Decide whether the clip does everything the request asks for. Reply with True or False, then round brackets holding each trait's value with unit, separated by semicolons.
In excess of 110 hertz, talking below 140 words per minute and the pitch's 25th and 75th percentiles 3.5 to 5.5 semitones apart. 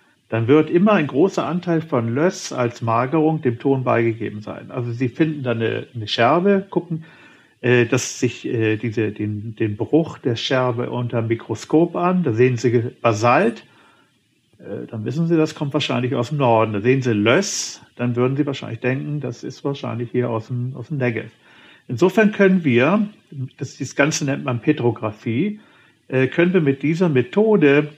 False (130 Hz; 170 wpm; 4.6 semitones)